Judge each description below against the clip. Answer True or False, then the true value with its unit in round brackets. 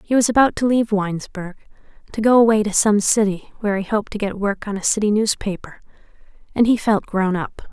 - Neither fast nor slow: False (210 wpm)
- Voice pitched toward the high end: True (210 Hz)